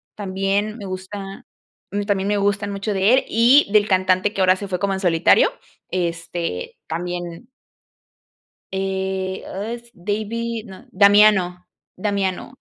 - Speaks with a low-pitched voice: No, high, 195 Hz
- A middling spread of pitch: No, narrow, 1.9 semitones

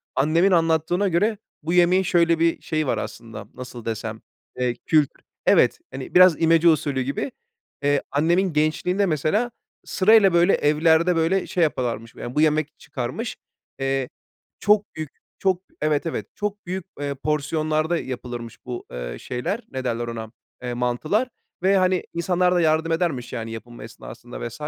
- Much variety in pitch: Yes, wide, 5.7 semitones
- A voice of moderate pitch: Yes, medium, 155 Hz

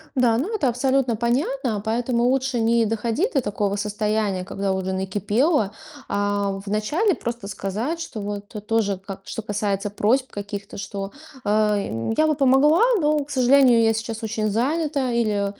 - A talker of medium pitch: No, high, 225 Hz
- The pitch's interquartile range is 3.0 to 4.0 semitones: No, average, 4.4 semitones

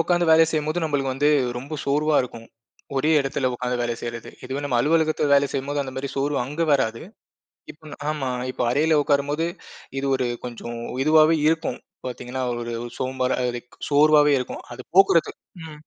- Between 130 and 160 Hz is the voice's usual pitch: Yes, medium, 140 Hz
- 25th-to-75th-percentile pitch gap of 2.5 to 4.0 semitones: Yes, average, 3.3 semitones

